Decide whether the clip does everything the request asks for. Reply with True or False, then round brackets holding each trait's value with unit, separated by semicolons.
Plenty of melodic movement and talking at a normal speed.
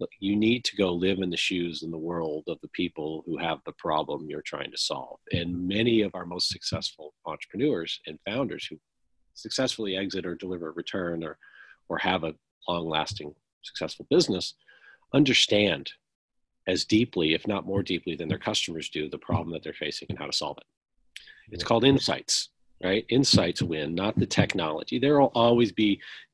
False (4.1 semitones; 180 wpm)